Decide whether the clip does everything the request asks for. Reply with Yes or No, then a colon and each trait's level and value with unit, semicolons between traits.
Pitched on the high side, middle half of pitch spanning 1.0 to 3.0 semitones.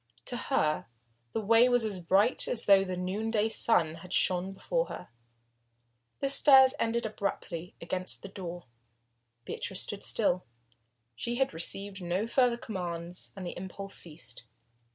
No: high, 195 Hz; average, 4.2 semitones